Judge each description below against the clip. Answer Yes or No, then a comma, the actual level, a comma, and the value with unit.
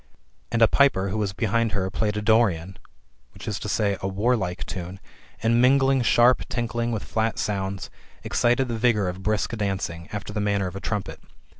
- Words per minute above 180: No, average, 170 wpm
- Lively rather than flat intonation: No, average, 3.3 semitones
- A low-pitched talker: Yes, low, 105 Hz